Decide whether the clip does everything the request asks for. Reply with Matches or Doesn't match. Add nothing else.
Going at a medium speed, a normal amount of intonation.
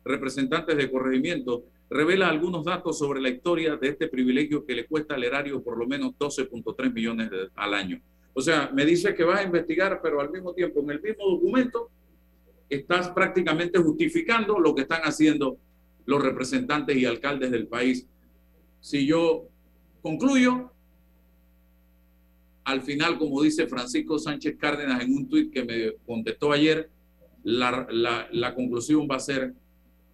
Doesn't match